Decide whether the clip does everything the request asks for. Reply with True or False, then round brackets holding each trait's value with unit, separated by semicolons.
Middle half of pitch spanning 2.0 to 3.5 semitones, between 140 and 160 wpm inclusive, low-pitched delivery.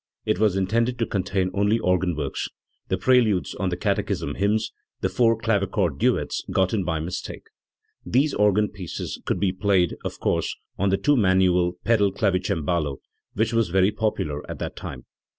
False (3.1 semitones; 170 wpm; 95 Hz)